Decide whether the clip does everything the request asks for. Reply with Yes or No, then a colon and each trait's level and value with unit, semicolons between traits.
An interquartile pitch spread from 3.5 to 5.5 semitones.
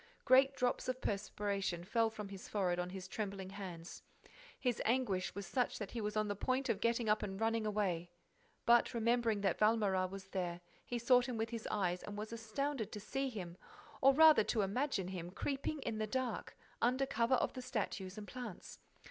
Yes: average, 4.0 semitones